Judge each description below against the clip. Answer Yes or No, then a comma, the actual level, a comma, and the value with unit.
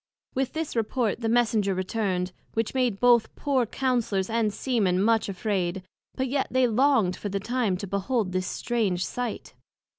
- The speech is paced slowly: No, average, 175 wpm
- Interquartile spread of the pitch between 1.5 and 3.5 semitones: No, average, 4.3 semitones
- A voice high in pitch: Yes, high, 225 Hz